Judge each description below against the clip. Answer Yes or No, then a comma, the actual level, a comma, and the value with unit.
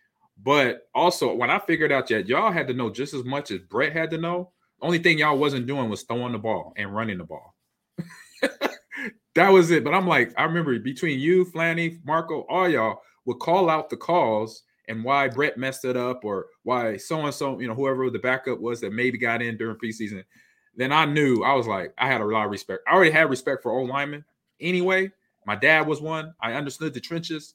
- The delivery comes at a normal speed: No, fast, 225 wpm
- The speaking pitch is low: No, medium, 145 Hz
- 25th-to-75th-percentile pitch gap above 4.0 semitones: Yes, average, 5.0 semitones